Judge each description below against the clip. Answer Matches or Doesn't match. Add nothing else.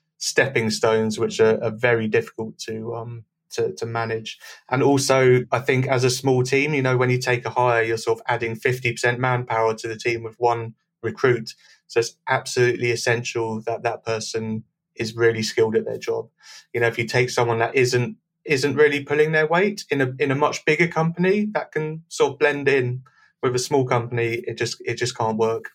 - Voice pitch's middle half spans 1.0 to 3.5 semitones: Doesn't match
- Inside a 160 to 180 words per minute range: Doesn't match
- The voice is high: Doesn't match